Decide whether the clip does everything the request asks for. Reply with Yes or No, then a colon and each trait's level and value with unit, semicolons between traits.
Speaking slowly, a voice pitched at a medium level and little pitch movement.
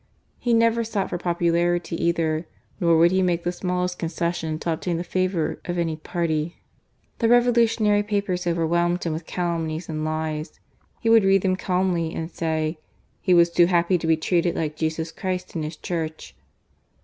No: average, 175 wpm; medium, 170 Hz; narrow, 2.2 semitones